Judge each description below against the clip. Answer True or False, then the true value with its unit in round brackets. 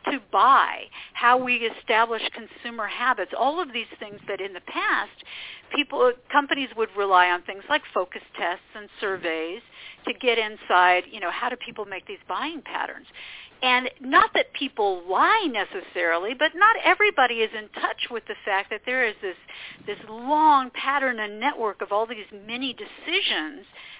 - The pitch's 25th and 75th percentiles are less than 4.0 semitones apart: False (4.9 semitones)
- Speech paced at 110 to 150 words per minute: False (170 wpm)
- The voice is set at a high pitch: True (225 Hz)